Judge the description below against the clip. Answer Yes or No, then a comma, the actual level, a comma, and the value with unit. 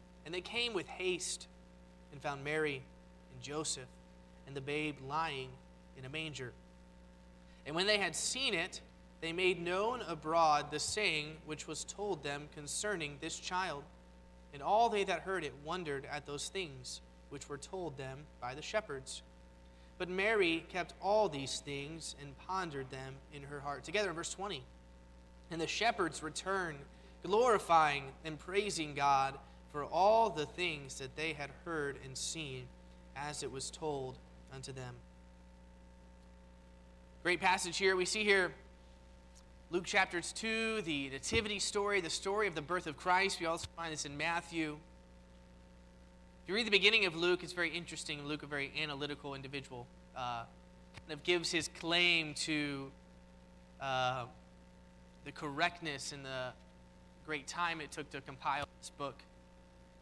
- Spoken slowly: No, average, 155 wpm